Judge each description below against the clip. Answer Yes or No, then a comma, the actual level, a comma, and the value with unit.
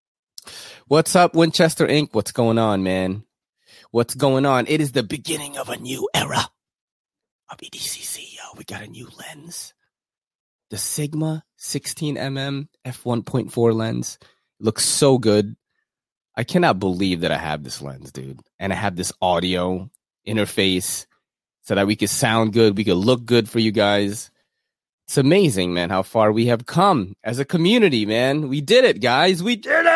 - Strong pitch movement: Yes, wide, 6.7 semitones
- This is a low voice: Yes, low, 115 Hz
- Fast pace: No, average, 170 wpm